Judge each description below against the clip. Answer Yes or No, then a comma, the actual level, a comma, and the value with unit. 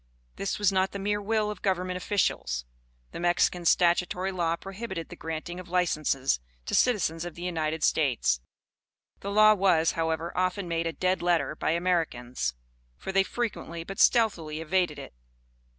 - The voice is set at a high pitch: No, medium, 175 Hz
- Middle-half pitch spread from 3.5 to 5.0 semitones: No, average, 3.0 semitones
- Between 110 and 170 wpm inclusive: Yes, average, 160 wpm